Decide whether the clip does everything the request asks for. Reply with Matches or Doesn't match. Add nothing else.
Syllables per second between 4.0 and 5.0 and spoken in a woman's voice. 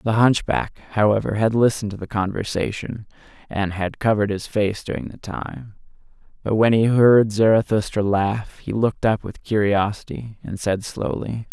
Doesn't match